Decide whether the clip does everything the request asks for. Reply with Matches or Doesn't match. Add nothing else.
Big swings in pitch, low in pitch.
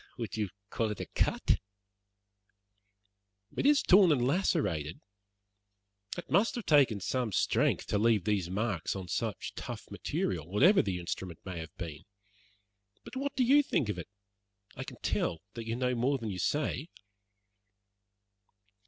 Matches